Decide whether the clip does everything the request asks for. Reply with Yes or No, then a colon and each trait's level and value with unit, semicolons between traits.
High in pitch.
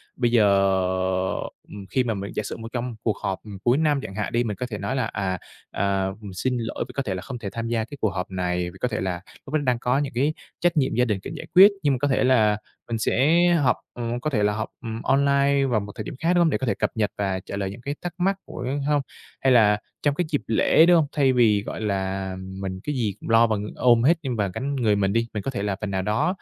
No: low, 115 Hz